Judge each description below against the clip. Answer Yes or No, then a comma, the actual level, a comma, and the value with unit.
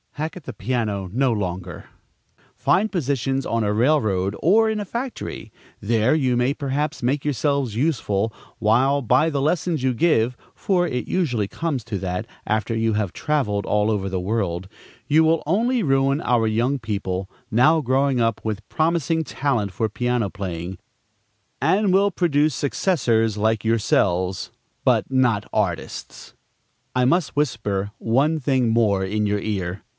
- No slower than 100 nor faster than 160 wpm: Yes, average, 150 wpm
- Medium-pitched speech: No, low, 125 Hz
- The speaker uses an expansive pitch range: Yes, wide, 6.0 semitones